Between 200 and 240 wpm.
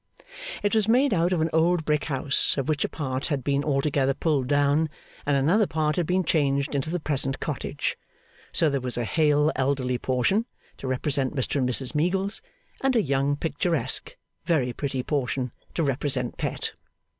No: average, 180 wpm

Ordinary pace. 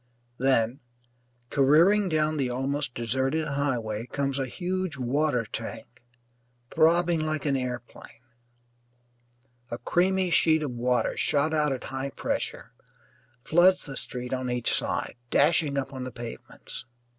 No: slow, 130 wpm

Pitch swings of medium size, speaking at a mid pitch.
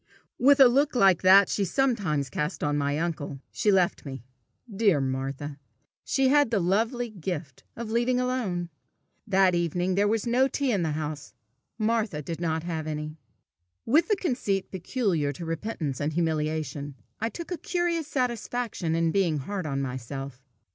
No: wide, 7.6 semitones; medium, 180 Hz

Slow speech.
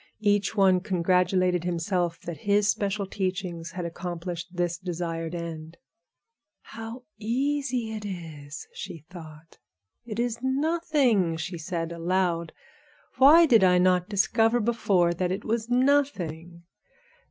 Yes: slow, 120 wpm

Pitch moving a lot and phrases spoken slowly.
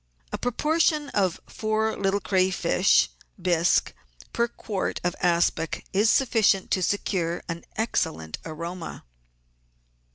No: average, 4.3 semitones; slow, 110 wpm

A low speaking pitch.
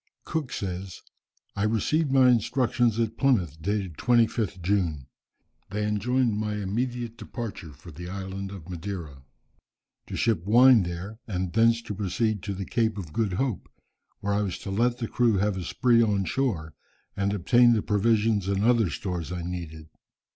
Yes: low, 105 Hz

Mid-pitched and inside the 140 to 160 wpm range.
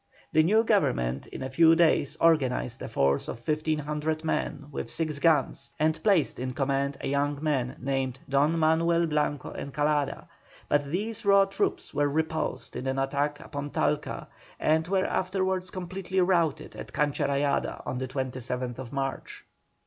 Yes: medium, 150 Hz; average, 155 wpm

